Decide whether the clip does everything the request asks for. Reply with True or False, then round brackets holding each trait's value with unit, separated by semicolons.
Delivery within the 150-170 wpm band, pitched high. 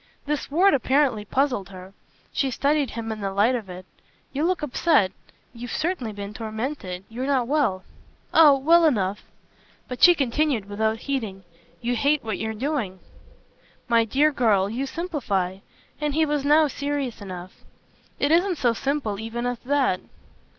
True (155 wpm; 250 Hz)